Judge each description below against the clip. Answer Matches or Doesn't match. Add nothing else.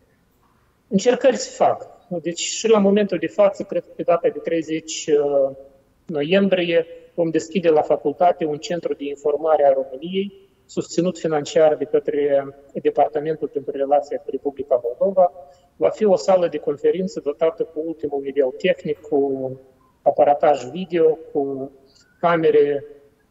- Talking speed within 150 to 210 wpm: Doesn't match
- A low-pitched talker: Doesn't match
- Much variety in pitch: Doesn't match